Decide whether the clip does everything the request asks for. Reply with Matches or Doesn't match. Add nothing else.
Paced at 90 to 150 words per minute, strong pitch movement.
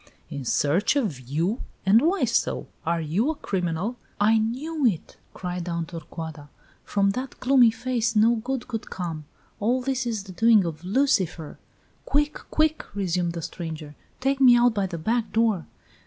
Doesn't match